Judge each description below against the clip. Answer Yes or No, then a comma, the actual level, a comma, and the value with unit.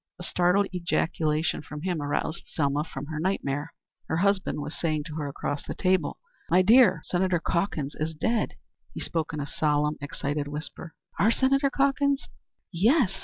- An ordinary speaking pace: Yes, average, 165 wpm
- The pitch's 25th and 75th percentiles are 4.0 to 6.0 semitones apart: Yes, average, 4.5 semitones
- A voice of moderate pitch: Yes, medium, 165 Hz